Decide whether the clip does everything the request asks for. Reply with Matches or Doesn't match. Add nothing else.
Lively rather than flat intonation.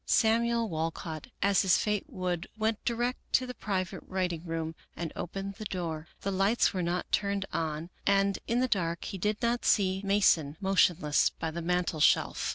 Doesn't match